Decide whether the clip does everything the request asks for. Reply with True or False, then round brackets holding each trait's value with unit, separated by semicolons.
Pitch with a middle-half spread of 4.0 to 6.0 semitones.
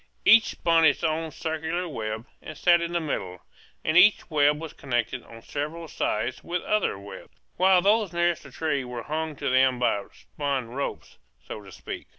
True (5.1 semitones)